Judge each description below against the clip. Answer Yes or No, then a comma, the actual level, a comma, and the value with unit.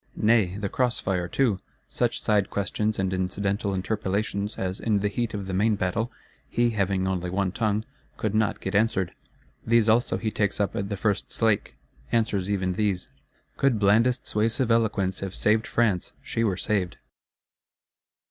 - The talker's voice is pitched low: Yes, low, 105 Hz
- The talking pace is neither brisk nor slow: Yes, average, 165 wpm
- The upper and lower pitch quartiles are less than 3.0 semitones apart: Yes, narrow, 2.6 semitones